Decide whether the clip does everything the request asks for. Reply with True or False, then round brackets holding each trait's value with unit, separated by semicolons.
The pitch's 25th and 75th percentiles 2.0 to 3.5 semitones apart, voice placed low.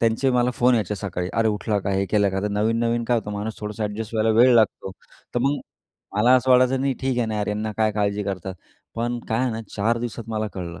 True (2.6 semitones; 110 Hz)